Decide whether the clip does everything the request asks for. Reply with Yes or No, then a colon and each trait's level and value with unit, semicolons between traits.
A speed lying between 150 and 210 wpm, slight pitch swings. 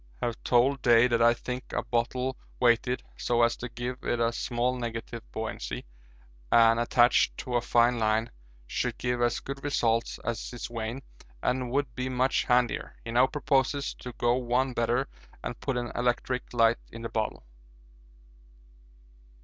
Yes: average, 160 wpm; narrow, 1.4 semitones